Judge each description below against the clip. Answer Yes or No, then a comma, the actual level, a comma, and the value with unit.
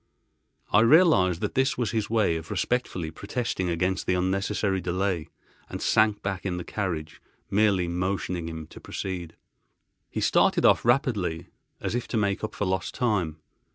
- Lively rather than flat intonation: No, average, 3.6 semitones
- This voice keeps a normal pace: Yes, average, 160 wpm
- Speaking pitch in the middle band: No, very low, 95 Hz